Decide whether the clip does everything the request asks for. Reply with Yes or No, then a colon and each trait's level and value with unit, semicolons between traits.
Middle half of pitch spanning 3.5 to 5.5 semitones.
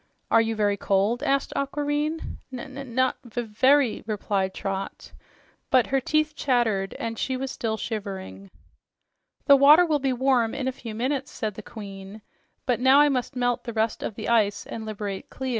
Yes: average, 4.1 semitones